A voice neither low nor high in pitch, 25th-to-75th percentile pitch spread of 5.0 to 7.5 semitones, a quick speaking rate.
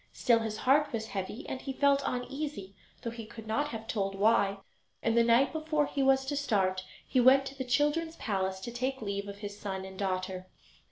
No: high, 230 Hz; average, 5.3 semitones; fast, 210 wpm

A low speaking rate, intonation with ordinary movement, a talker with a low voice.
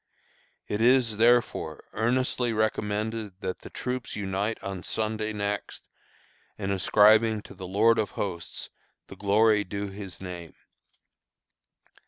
No: slow, 120 wpm; narrow, 2.3 semitones; low, 105 Hz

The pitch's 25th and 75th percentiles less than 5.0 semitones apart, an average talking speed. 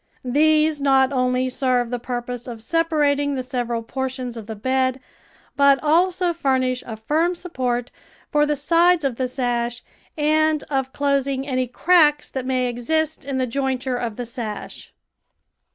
Yes: average, 3.2 semitones; average, 165 wpm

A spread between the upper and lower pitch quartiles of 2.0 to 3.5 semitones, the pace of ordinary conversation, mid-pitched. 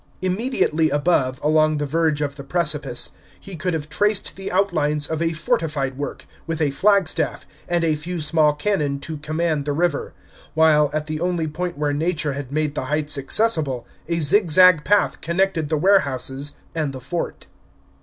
Yes: average, 3.0 semitones; average, 170 wpm; medium, 155 Hz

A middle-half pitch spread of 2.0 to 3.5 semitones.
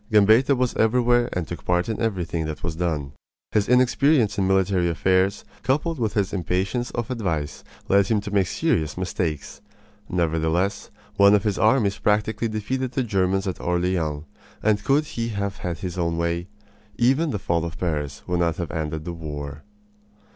No: average, 4.7 semitones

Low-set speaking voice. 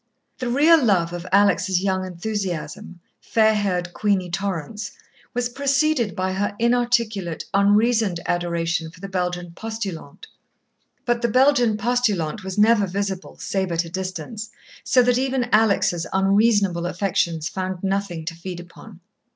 No: high, 195 Hz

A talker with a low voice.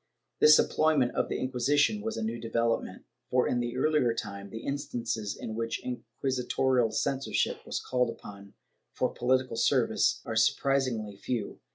Yes: low, 125 Hz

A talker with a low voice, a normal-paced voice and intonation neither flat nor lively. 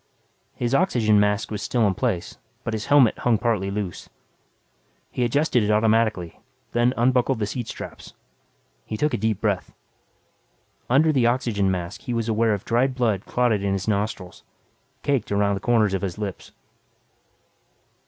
Yes: low, 110 Hz; average, 160 wpm; average, 3.2 semitones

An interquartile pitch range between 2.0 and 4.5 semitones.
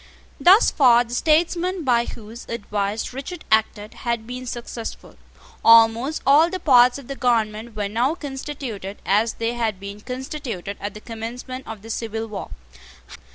Yes: average, 3.4 semitones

